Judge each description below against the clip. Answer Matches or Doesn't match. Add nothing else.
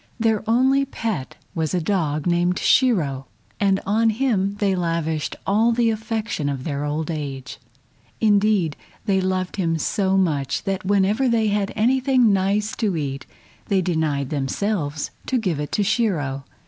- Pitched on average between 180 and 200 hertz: Matches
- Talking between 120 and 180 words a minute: Matches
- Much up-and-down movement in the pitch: Matches